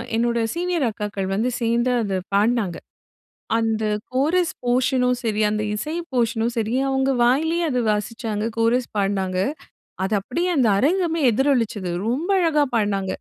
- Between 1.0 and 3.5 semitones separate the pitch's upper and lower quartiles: No, average, 4.2 semitones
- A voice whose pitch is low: No, high, 235 Hz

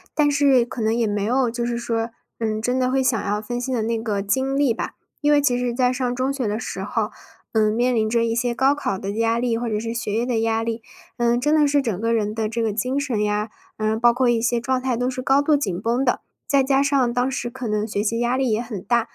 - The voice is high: Yes, high, 240 Hz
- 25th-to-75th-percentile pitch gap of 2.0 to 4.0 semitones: Yes, narrow, 2.6 semitones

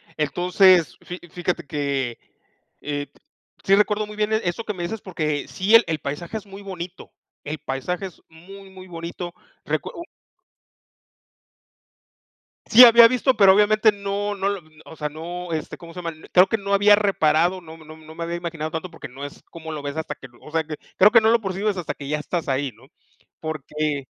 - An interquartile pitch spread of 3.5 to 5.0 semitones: Yes, average, 4.2 semitones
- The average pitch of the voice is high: No, medium, 175 Hz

